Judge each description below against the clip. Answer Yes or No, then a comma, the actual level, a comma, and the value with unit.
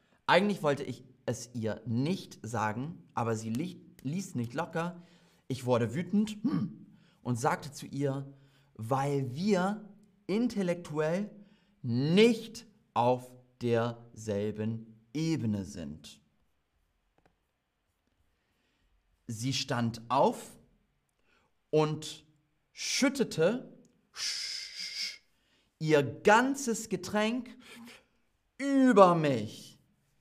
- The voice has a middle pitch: Yes, medium, 150 Hz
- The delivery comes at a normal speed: No, slow, 75 wpm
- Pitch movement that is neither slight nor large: No, wide, 8.4 semitones